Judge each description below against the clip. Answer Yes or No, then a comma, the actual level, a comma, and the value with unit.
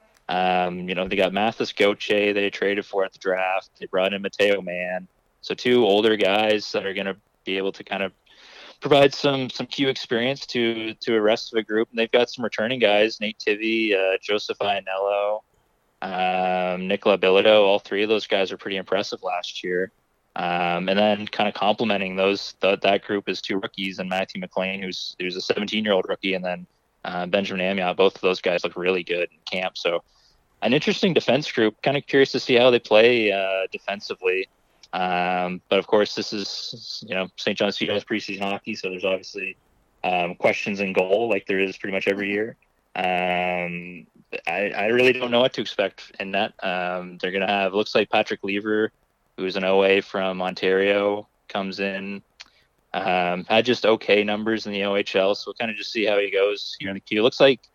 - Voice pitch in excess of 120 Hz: No, low, 100 Hz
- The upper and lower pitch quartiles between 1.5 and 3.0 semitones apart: Yes, average, 2.7 semitones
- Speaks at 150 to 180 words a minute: No, average, 200 wpm